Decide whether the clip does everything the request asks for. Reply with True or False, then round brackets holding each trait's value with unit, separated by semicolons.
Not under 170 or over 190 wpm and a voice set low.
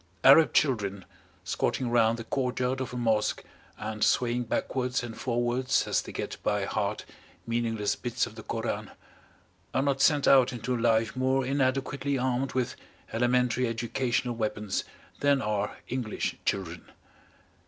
False (140 wpm; 125 Hz)